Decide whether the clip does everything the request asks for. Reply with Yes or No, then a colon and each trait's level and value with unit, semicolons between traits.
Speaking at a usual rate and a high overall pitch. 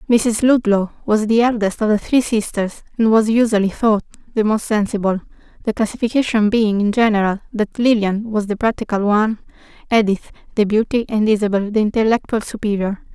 Yes: average, 160 wpm; high, 215 Hz